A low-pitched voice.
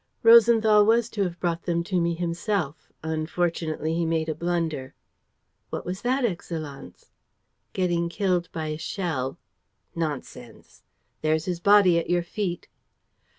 No: medium, 170 Hz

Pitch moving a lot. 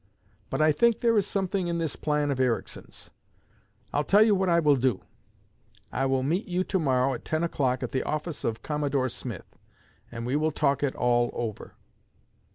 No: average, 4.8 semitones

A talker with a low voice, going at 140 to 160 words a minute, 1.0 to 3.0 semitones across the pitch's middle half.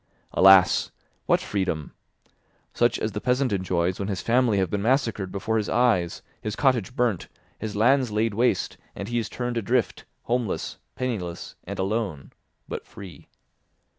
No: low, 110 Hz; average, 150 wpm; average, 4.2 semitones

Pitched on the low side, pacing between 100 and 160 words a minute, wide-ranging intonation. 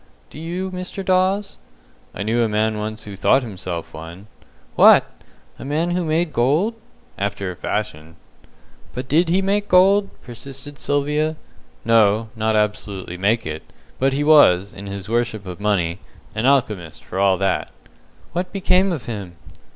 Yes: low, 115 Hz; average, 155 wpm; wide, 8.4 semitones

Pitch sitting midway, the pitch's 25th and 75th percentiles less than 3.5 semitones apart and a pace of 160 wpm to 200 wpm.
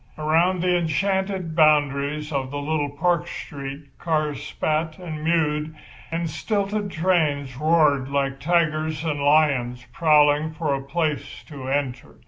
No: medium, 155 Hz; average, 2.8 semitones; slow, 135 wpm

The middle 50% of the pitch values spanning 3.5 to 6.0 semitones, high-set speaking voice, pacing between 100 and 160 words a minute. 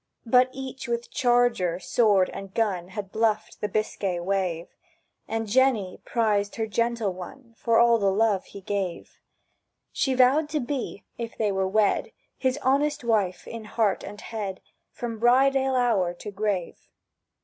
Yes: average, 3.8 semitones; high, 220 Hz; average, 155 wpm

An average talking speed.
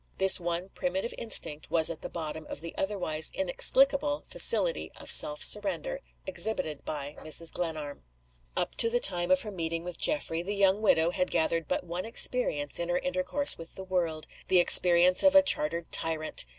Yes: average, 175 wpm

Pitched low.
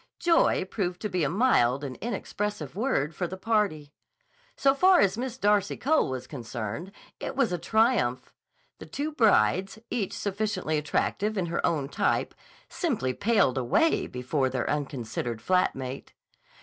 No: medium, 185 Hz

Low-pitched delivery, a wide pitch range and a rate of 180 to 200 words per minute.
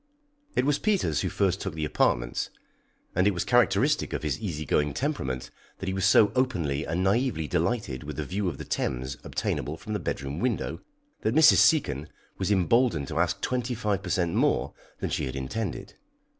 Yes: very low, 90 Hz; wide, 6.9 semitones; average, 190 wpm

